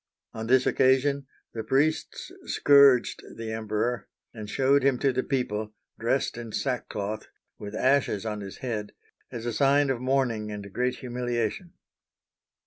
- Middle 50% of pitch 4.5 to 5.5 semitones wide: No, average, 3.7 semitones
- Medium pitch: No, low, 120 Hz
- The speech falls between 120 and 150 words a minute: Yes, average, 140 wpm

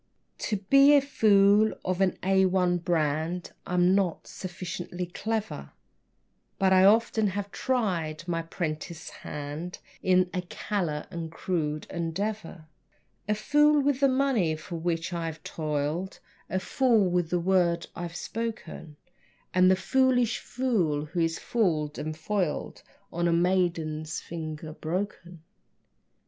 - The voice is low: No, medium, 180 Hz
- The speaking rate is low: Yes, slow, 130 wpm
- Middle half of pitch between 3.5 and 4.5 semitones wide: Yes, average, 3.8 semitones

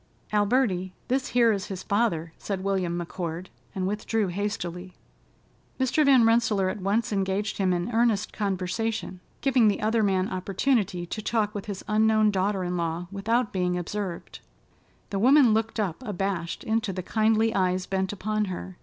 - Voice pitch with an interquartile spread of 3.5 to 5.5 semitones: No, average, 3.0 semitones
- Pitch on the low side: No, high, 200 Hz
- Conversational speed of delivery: Yes, average, 160 wpm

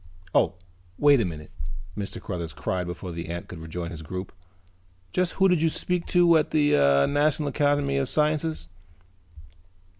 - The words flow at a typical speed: Yes, average, 155 wpm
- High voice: No, low, 135 Hz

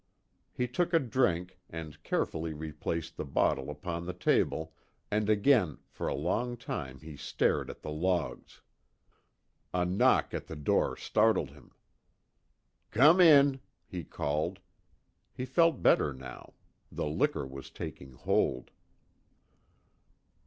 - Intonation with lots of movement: Yes, wide, 7.7 semitones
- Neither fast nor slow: No, slow, 125 wpm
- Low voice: Yes, very low, 85 Hz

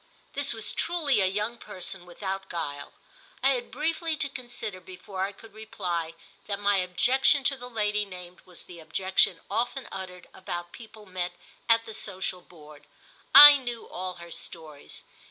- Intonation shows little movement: No, average, 5.0 semitones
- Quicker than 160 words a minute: No, average, 155 wpm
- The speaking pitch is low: No, high, 195 Hz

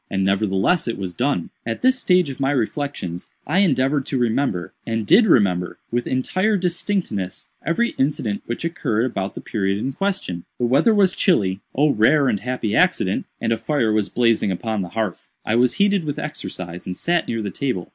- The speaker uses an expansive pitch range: Yes, wide, 7.3 semitones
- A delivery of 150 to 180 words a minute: No, average, 190 wpm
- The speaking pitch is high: No, low, 120 Hz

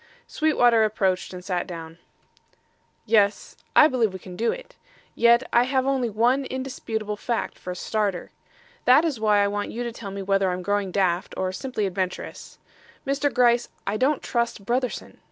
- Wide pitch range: No, average, 4.4 semitones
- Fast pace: No, average, 170 wpm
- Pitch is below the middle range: No, high, 220 Hz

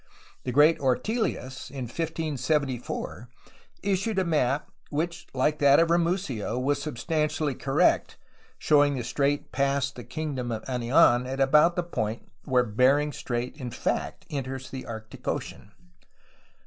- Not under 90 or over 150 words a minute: Yes, slow, 135 wpm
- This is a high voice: No, medium, 140 Hz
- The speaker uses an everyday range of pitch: Yes, average, 3.6 semitones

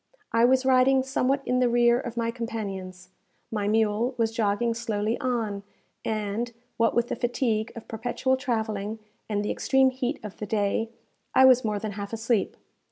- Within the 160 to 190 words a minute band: Yes, average, 170 wpm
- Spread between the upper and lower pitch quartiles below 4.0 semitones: Yes, average, 2.9 semitones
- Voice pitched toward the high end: Yes, high, 230 Hz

